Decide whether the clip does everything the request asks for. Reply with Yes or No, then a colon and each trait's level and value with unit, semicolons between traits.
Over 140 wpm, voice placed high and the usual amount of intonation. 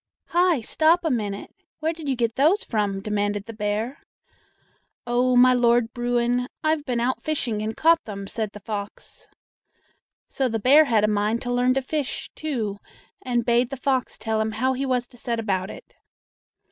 Yes: average, 185 wpm; high, 240 Hz; average, 3.6 semitones